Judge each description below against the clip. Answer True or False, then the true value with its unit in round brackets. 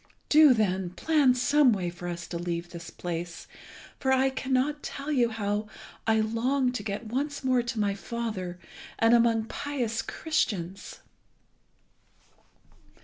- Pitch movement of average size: False (5.8 semitones)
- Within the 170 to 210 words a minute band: False (140 wpm)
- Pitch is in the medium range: False (225 Hz)